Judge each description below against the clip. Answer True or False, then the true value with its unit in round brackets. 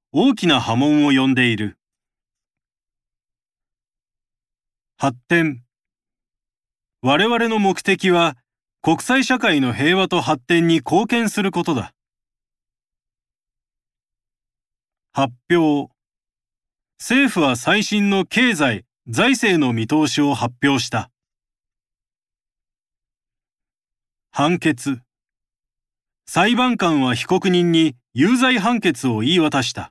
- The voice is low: False (145 Hz)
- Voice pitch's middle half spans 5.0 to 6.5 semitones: False (7.8 semitones)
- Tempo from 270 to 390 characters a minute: False (155 characters per minute)